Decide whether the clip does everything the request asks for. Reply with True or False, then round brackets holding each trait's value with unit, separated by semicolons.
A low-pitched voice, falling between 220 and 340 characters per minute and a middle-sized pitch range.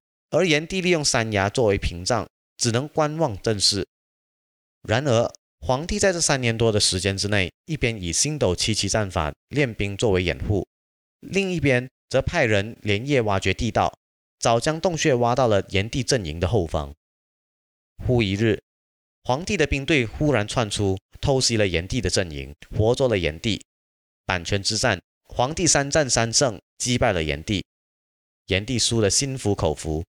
False (105 Hz; 240 characters per minute; 6.1 semitones)